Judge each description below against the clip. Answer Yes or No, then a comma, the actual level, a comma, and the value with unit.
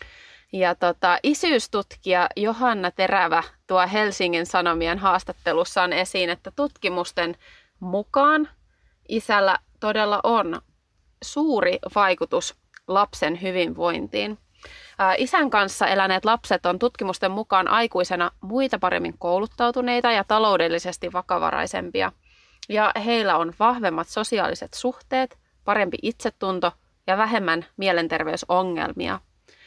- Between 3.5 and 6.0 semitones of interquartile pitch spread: Yes, average, 4.1 semitones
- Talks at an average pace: No, slow, 90 wpm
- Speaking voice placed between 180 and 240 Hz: Yes, high, 190 Hz